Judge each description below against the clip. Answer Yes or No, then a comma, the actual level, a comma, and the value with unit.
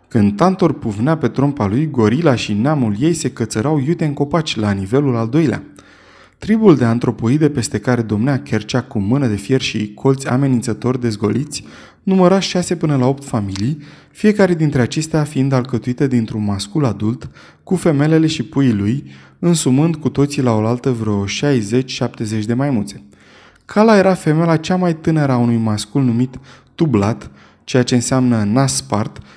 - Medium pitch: No, low, 130 Hz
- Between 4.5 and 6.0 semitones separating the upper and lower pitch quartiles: Yes, average, 5.1 semitones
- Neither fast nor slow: Yes, average, 155 wpm